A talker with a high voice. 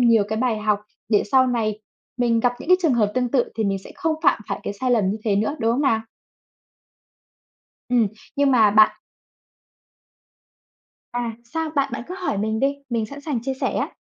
Yes: high, 235 Hz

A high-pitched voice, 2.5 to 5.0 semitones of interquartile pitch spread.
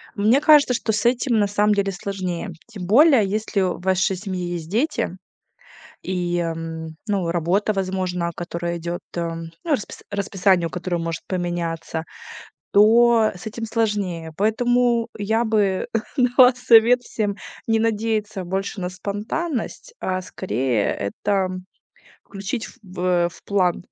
Yes: high, 195 Hz; average, 4.0 semitones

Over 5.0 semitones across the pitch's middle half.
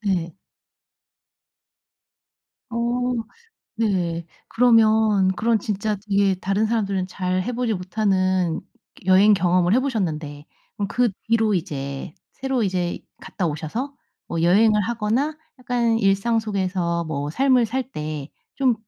No: average, 4.3 semitones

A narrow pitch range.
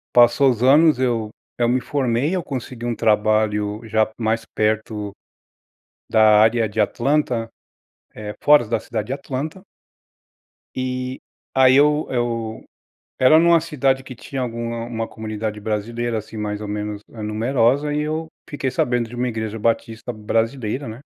No: average, 3.2 semitones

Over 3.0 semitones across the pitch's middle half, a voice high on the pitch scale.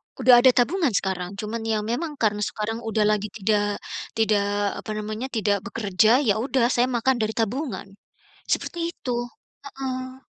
Yes: average, 3.7 semitones; high, 225 Hz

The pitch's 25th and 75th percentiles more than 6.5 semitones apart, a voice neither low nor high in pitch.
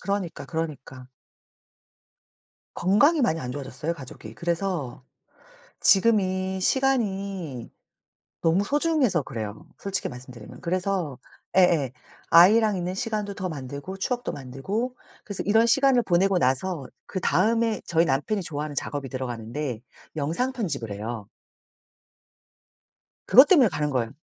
Yes: wide, 7.0 semitones; medium, 175 Hz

